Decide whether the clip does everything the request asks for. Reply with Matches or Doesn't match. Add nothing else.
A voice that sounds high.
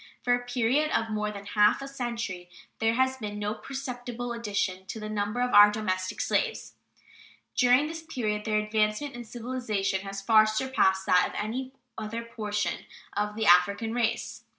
Matches